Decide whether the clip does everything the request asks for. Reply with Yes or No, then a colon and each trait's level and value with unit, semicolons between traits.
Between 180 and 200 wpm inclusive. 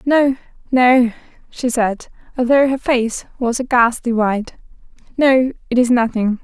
No: average, 140 wpm